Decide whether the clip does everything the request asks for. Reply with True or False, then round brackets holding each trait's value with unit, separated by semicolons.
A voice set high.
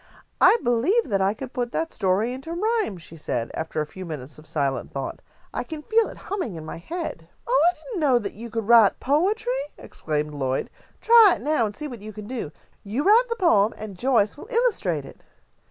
True (235 Hz)